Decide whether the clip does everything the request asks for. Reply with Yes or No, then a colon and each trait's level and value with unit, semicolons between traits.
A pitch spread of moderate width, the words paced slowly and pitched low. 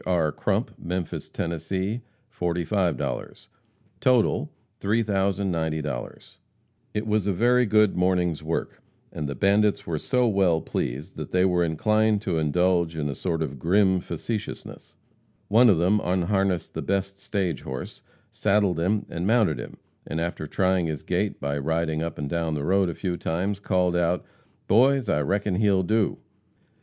No: average, 3.8 semitones; average, 155 wpm; very low, 90 Hz